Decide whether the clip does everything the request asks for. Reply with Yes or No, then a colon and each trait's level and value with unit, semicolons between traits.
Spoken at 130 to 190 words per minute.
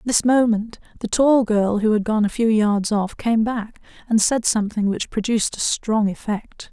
No: fast, 205 wpm